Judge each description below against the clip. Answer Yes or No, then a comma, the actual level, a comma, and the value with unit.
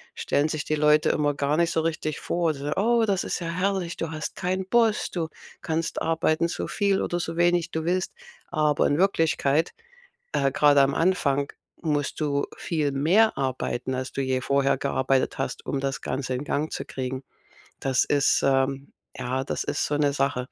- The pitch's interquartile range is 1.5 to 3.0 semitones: No, average, 3.5 semitones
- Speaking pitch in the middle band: Yes, medium, 150 Hz